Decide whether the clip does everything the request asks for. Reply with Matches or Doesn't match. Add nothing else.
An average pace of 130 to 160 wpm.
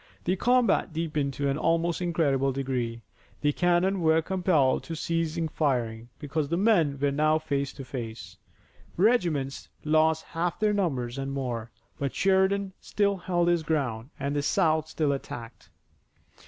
Matches